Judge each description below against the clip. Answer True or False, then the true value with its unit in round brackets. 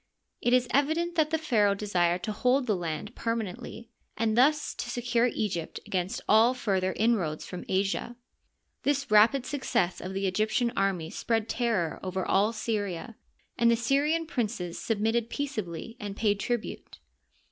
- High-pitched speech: True (220 Hz)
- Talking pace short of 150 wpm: False (160 wpm)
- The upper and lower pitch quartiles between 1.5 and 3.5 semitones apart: False (4.2 semitones)